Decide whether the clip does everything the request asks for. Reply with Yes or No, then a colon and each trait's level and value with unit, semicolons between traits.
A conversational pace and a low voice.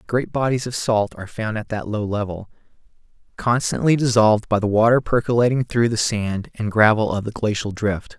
Yes: average, 185 wpm; low, 110 Hz